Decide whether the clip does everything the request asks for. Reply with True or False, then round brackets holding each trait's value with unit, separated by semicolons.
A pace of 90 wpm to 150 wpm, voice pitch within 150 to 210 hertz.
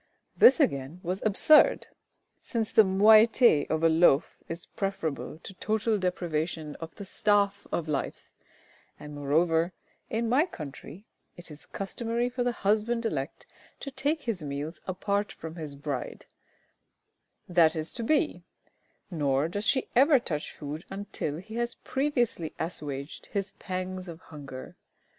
True (140 wpm; 185 Hz)